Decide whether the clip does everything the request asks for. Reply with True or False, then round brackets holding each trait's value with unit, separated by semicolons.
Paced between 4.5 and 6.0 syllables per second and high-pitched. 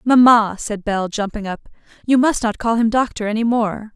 True (5.0 syllables/s; 220 Hz)